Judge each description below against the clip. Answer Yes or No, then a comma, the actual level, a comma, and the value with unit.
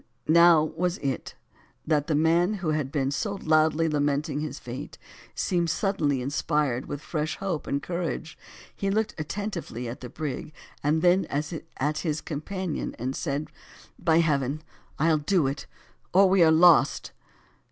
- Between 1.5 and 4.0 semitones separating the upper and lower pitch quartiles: Yes, average, 3.4 semitones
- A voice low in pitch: No, medium, 155 Hz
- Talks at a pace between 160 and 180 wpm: No, average, 145 wpm